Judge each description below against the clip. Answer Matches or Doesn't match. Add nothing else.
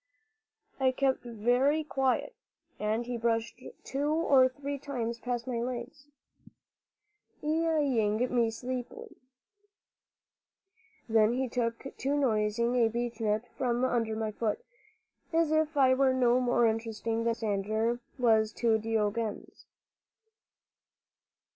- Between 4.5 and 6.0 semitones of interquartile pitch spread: Doesn't match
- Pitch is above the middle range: Matches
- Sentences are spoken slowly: Matches